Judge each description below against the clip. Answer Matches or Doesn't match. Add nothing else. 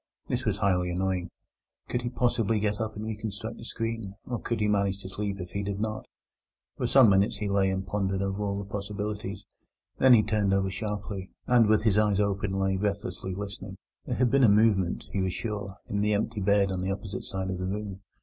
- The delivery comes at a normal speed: Doesn't match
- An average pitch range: Doesn't match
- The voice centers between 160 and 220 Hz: Doesn't match